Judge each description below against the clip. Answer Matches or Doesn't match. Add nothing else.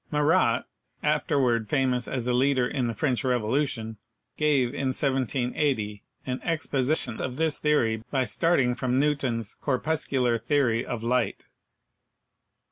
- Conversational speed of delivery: Doesn't match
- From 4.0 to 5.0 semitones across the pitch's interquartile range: Doesn't match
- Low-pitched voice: Matches